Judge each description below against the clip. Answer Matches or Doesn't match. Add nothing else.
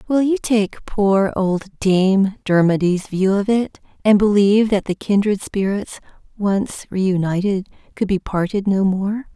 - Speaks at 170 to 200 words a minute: Doesn't match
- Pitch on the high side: Matches